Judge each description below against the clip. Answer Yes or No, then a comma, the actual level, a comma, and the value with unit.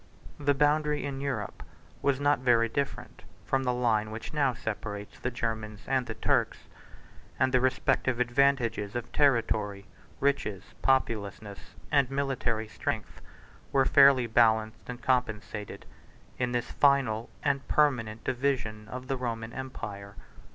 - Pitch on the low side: Yes, low, 125 Hz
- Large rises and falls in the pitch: No, average, 3.7 semitones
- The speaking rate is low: Yes, slow, 130 wpm